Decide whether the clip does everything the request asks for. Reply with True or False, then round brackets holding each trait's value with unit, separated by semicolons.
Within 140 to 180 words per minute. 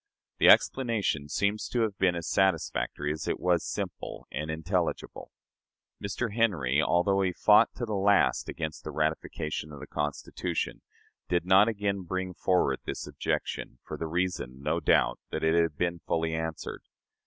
True (160 wpm)